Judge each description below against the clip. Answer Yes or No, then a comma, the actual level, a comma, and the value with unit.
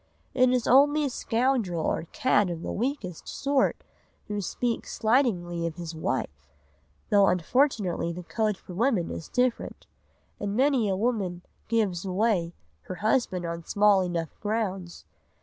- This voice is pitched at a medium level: No, high, 205 Hz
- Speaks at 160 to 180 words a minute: No, average, 145 wpm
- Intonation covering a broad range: Yes, wide, 5.9 semitones